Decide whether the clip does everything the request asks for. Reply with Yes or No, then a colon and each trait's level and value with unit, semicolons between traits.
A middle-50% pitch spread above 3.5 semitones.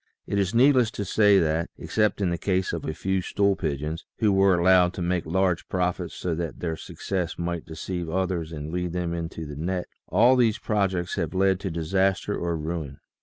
No: narrow, 2.6 semitones